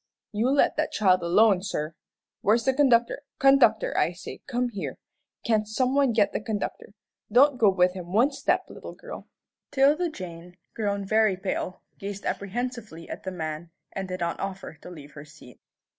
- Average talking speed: Yes, average, 175 wpm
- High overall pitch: Yes, high, 205 Hz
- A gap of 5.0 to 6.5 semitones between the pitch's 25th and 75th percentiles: Yes, average, 5.3 semitones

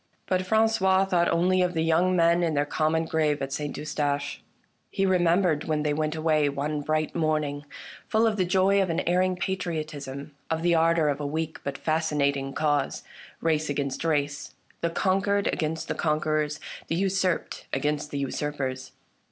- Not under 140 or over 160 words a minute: No, average, 170 wpm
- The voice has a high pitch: No, medium, 160 Hz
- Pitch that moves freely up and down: No, average, 3.3 semitones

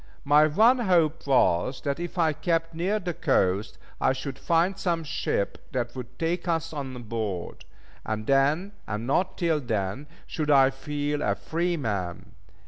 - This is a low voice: No, medium, 145 Hz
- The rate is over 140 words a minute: Yes, average, 160 wpm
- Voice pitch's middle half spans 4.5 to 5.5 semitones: Yes, average, 5.2 semitones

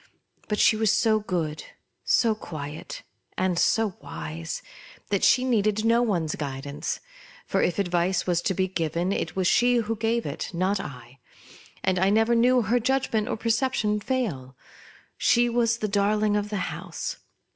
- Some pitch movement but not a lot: Yes, average, 4.6 semitones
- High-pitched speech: Yes, high, 205 Hz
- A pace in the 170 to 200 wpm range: No, average, 160 wpm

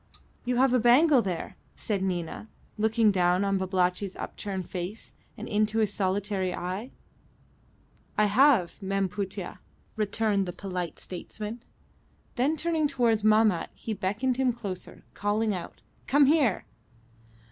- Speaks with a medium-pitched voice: No, high, 210 Hz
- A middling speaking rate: No, slow, 130 wpm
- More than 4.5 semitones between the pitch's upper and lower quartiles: No, average, 3.9 semitones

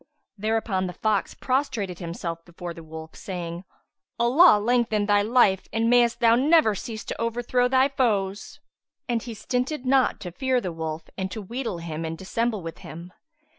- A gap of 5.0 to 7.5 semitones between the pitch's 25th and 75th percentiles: Yes, average, 5.3 semitones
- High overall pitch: Yes, high, 215 Hz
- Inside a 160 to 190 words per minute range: Yes, average, 170 wpm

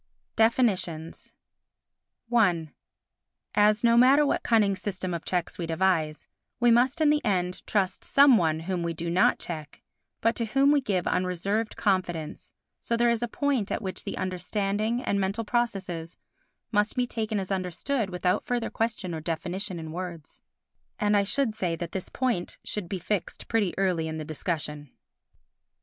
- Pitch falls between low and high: No, high, 195 Hz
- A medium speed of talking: Yes, average, 165 wpm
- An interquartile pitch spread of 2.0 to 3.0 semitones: No, average, 4.8 semitones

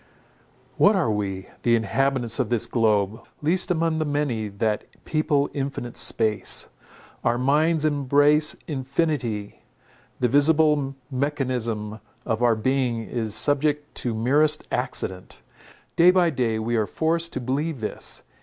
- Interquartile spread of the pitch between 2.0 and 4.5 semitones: No, average, 5.0 semitones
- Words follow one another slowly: Yes, slow, 130 wpm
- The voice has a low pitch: Yes, low, 130 Hz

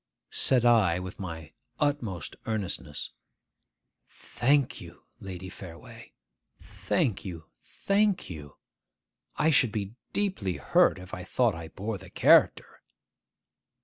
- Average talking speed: No, slow, 115 wpm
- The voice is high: No, low, 100 Hz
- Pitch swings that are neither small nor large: No, wide, 5.8 semitones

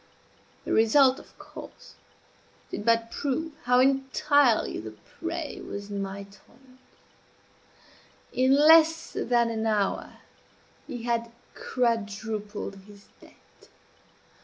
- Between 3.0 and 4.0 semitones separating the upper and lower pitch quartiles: No, average, 4.6 semitones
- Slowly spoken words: Yes, slow, 105 wpm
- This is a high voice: Yes, high, 235 Hz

